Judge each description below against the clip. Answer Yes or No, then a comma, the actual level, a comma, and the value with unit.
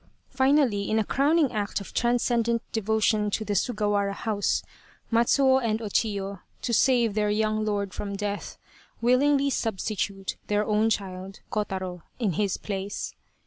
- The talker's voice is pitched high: Yes, high, 215 Hz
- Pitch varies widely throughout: No, average, 2.8 semitones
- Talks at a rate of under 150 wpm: Yes, average, 140 wpm